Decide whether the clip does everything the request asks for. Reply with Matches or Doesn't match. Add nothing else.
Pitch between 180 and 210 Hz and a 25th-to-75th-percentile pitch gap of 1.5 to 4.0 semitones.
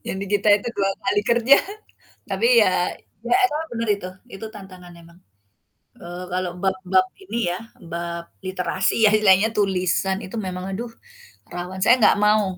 Matches